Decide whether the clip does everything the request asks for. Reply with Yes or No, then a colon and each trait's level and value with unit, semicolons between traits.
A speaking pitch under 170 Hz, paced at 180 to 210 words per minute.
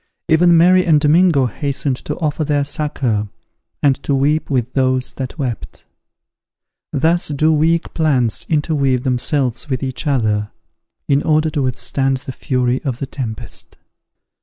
No: medium, 140 Hz; average, 140 wpm